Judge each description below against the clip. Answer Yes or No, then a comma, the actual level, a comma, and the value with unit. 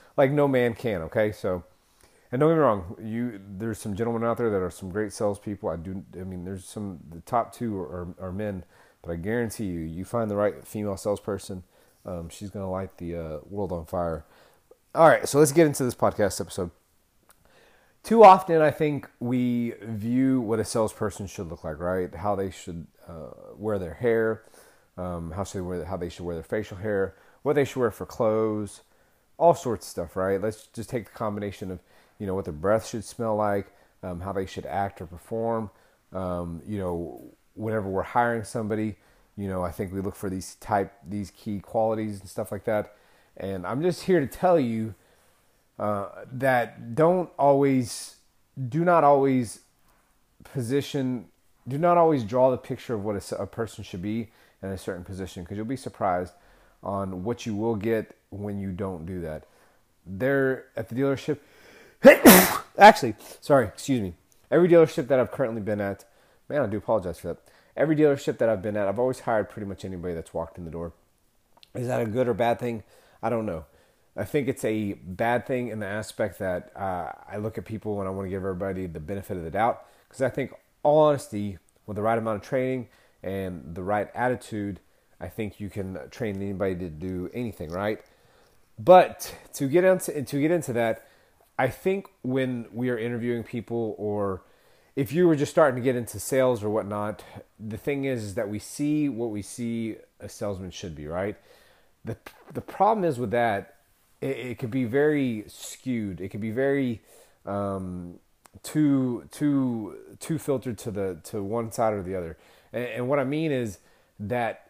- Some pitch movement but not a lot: Yes, average, 4.5 semitones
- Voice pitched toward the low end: Yes, low, 105 Hz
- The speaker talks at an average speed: Yes, average, 195 wpm